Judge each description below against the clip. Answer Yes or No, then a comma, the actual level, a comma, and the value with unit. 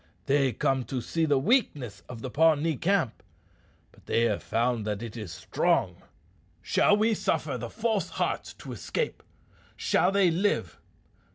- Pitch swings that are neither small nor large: No, wide, 8.3 semitones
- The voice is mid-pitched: Yes, medium, 145 Hz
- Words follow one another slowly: No, average, 155 wpm